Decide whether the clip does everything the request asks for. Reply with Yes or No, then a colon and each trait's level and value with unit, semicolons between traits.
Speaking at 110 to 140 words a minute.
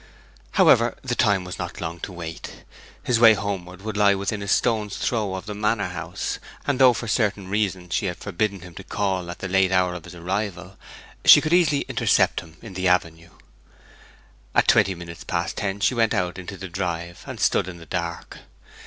No: average, 200 wpm